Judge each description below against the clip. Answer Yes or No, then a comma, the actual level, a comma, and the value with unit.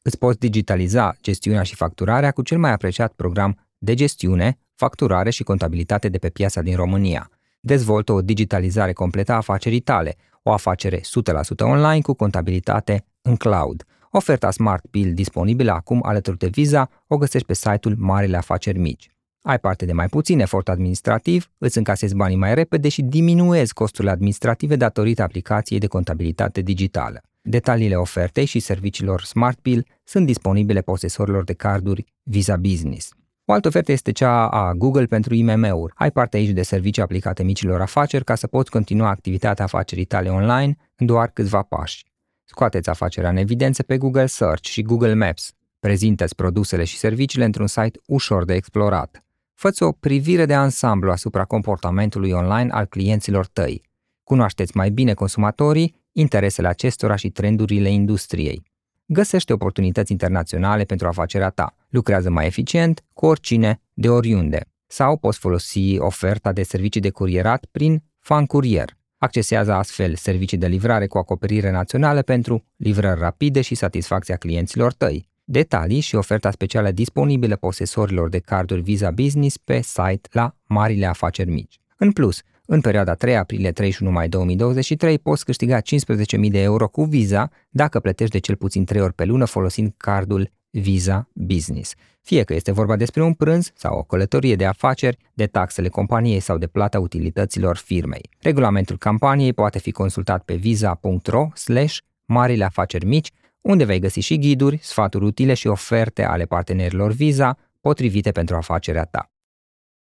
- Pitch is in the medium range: No, low, 105 Hz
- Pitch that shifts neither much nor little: Yes, average, 4.4 semitones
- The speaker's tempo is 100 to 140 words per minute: No, average, 155 wpm